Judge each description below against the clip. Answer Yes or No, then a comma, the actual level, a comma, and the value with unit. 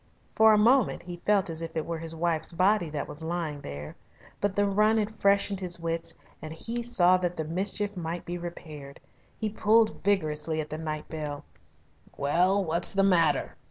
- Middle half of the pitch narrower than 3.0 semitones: No, average, 4.1 semitones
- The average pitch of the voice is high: No, medium, 175 Hz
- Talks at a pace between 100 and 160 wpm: No, average, 190 wpm